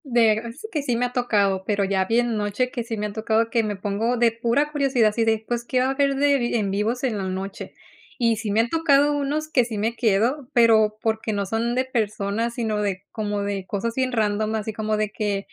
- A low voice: No, high, 225 Hz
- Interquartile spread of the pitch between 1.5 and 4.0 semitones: Yes, average, 2.9 semitones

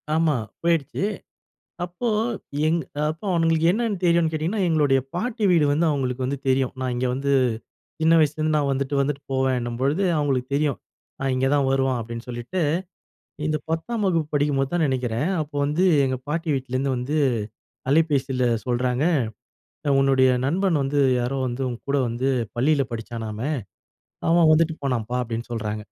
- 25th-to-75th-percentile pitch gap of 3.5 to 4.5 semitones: Yes, average, 3.9 semitones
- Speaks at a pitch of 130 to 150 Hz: Yes, medium, 140 Hz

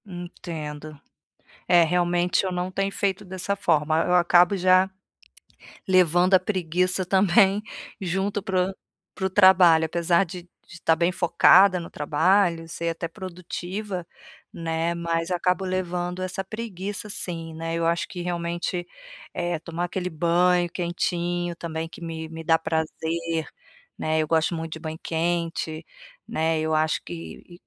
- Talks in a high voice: No, medium, 175 Hz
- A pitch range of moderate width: No, narrow, 2.0 semitones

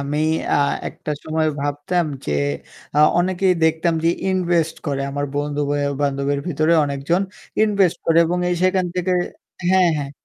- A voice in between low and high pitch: Yes, medium, 160 Hz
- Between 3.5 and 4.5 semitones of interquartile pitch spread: Yes, average, 3.8 semitones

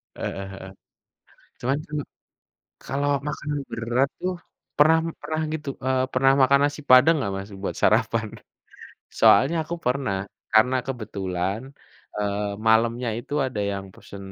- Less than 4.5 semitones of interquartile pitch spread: No, average, 5.2 semitones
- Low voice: Yes, low, 125 Hz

